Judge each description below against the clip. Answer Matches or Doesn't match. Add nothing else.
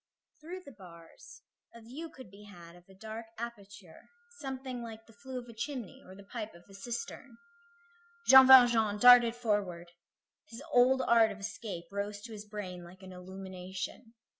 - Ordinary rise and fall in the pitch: Matches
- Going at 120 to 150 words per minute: Doesn't match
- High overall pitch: Matches